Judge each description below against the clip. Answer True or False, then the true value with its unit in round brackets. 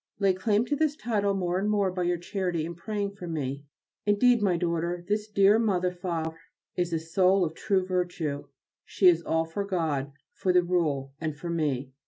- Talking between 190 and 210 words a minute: True (195 wpm)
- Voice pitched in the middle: True (180 Hz)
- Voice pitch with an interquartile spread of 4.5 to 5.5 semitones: False (3.5 semitones)